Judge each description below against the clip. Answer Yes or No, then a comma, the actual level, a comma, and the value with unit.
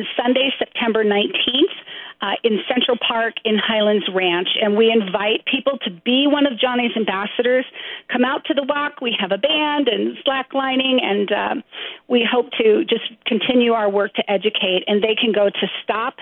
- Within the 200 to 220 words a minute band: No, average, 180 wpm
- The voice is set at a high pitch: Yes, high, 235 Hz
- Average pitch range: Yes, average, 3.8 semitones